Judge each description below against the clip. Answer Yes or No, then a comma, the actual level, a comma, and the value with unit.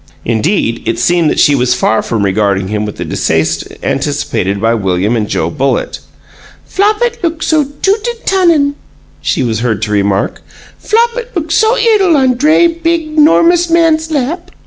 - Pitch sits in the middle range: No, very high, 270 Hz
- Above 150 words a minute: Yes, average, 165 wpm